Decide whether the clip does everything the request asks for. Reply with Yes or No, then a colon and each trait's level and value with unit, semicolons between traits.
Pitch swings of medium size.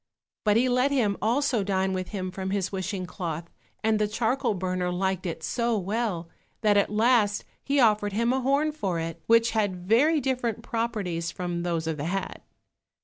Yes: average, 4.2 semitones